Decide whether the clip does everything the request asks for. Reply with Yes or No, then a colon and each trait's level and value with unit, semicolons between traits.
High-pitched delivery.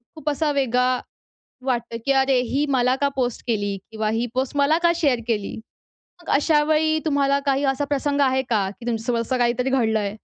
Yes: very high, 260 Hz